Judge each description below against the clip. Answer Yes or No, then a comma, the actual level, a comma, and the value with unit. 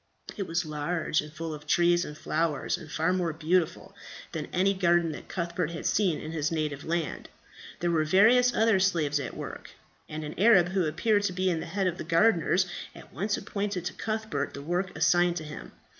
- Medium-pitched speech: Yes, medium, 170 Hz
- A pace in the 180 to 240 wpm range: Yes, average, 200 wpm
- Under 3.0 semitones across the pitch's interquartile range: No, average, 3.3 semitones